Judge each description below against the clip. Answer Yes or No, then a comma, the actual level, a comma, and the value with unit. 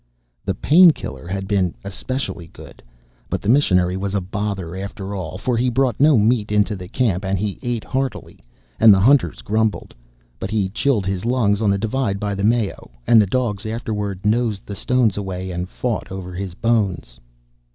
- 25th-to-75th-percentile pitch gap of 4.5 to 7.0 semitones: No, average, 3.5 semitones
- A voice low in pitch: Yes, low, 105 Hz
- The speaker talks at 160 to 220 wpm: Yes, average, 185 wpm